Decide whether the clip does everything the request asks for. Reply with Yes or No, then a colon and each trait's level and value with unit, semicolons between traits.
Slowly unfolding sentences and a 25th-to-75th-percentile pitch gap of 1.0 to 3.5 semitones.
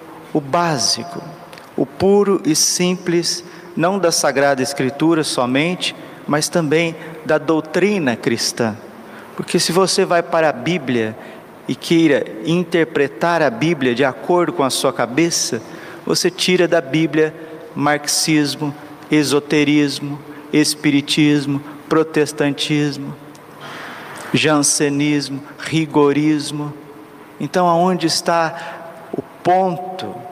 Yes: slow, 95 wpm; average, 2.8 semitones